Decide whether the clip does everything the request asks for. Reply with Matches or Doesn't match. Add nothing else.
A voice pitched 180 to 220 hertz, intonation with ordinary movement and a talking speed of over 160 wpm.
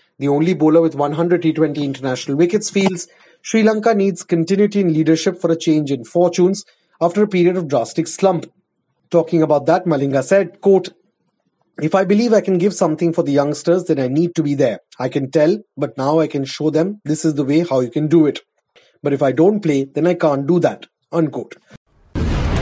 Doesn't match